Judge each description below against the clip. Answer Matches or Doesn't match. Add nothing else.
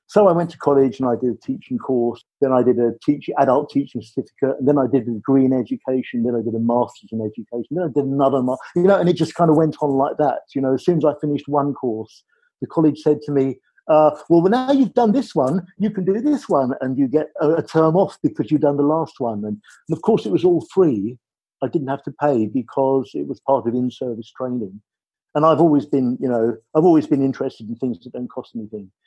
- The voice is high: Doesn't match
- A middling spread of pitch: Matches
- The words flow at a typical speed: Doesn't match